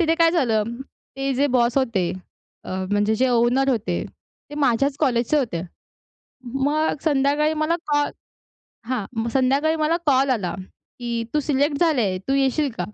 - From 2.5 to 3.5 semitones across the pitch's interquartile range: No, average, 3.9 semitones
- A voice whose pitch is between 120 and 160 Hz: No, very high, 270 Hz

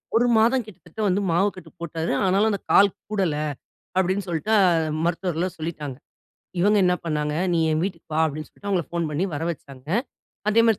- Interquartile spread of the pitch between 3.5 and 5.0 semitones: Yes, average, 4.2 semitones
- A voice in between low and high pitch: Yes, medium, 175 Hz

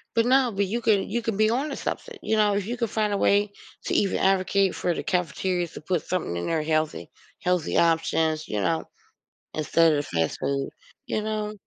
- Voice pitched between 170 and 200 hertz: Yes, high, 190 Hz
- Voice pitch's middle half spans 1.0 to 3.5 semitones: No, average, 5.1 semitones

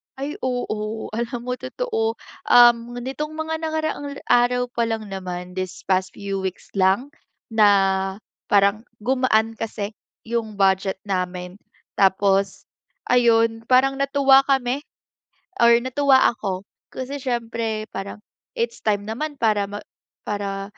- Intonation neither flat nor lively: Yes, average, 4.7 semitones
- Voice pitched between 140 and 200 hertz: No, high, 225 Hz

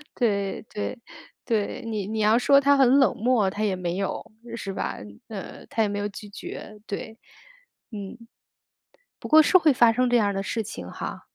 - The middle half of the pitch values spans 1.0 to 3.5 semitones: Yes, average, 3.2 semitones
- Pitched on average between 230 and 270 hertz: No, high, 215 Hz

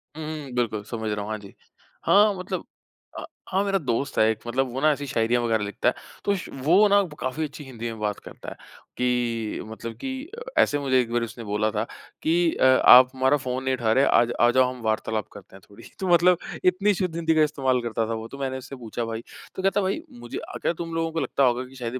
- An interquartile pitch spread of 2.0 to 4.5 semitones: No, wide, 5.6 semitones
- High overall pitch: No, low, 130 Hz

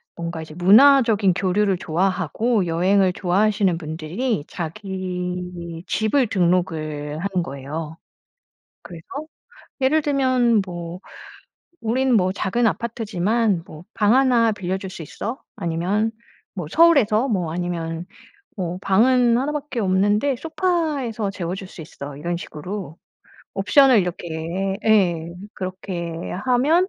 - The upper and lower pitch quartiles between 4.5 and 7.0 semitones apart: Yes, average, 5.1 semitones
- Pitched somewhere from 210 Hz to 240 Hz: No, high, 190 Hz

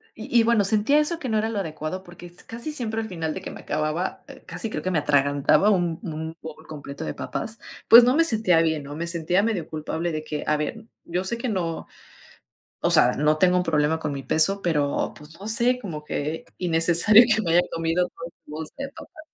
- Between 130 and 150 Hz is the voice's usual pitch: No, medium, 175 Hz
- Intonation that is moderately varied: No, wide, 5.8 semitones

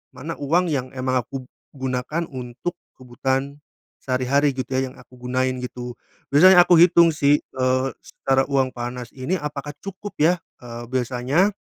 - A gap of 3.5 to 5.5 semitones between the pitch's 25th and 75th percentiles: No, average, 2.8 semitones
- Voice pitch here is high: No, low, 130 Hz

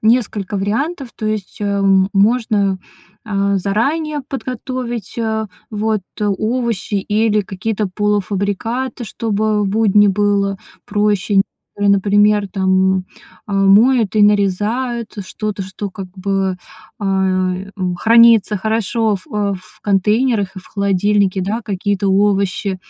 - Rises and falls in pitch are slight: Yes, narrow, 2.1 semitones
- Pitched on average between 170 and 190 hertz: No, high, 205 Hz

